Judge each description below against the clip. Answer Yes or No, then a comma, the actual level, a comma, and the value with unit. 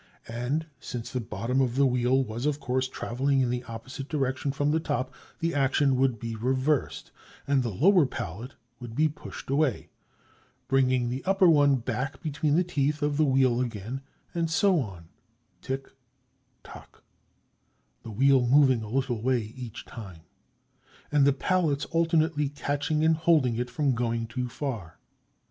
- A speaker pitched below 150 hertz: Yes, low, 135 Hz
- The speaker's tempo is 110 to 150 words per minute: No, average, 160 wpm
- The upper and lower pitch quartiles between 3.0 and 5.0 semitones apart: Yes, average, 3.3 semitones